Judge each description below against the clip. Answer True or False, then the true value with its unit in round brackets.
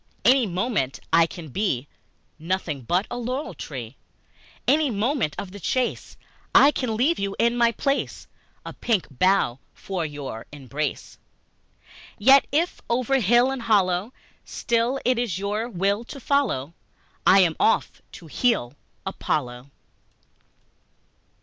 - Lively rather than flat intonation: True (7.3 semitones)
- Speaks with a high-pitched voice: True (205 Hz)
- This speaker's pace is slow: True (130 wpm)